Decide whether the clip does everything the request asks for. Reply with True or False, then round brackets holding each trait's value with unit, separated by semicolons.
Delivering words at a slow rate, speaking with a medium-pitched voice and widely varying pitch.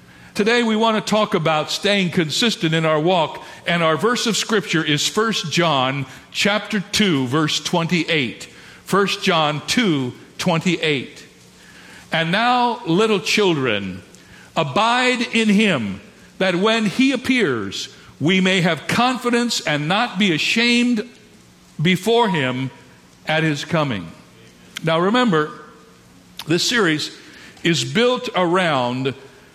True (120 wpm; 180 Hz; 6.0 semitones)